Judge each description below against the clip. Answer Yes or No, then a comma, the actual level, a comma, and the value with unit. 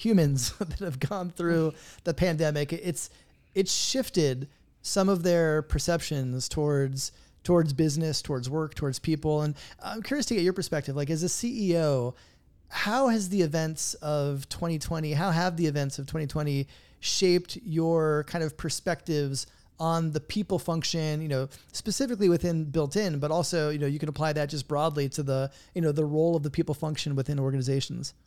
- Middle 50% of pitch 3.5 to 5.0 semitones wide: No, average, 3.1 semitones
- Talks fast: No, average, 170 wpm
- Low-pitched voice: No, medium, 155 Hz